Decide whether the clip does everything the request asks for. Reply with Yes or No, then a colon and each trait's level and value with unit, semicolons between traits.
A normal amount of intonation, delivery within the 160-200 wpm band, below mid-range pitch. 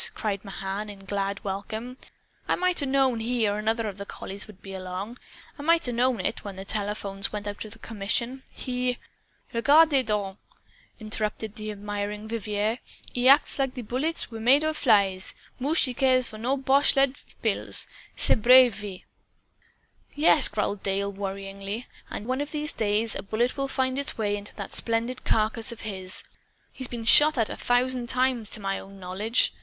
No: average, 4.0 semitones; average, 180 wpm; high, 220 Hz